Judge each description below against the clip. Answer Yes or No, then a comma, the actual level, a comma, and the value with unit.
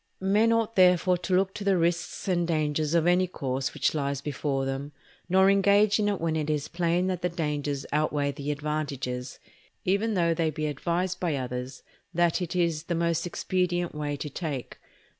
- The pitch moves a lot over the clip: No, average, 3.7 semitones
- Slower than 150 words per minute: No, average, 185 wpm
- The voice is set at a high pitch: No, medium, 165 Hz